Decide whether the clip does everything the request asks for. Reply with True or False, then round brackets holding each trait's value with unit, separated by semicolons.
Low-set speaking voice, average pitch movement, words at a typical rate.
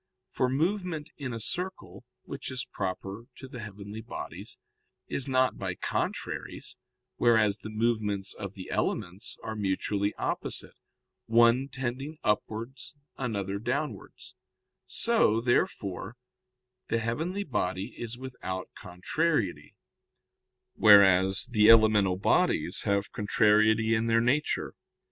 False (110 Hz; 4.2 semitones; 110 wpm)